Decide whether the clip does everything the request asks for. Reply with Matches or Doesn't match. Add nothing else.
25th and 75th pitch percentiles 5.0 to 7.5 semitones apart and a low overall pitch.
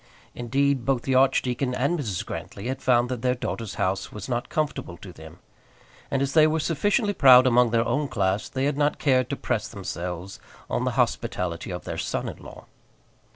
Matches